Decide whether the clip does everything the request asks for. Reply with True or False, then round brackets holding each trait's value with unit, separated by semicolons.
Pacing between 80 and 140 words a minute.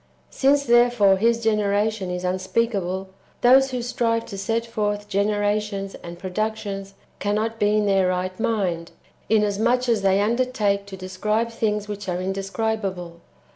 True (135 wpm)